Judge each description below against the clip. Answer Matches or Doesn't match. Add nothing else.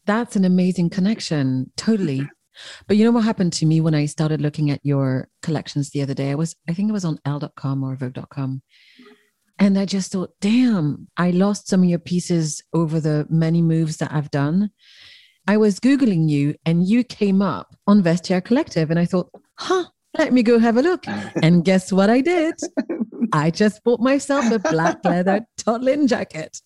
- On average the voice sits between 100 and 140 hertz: Doesn't match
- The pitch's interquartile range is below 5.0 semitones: Doesn't match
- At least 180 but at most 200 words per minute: Matches